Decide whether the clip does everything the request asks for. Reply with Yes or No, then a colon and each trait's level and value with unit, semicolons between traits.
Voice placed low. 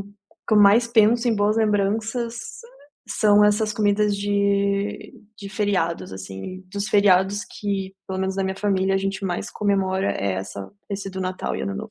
No: high, 200 Hz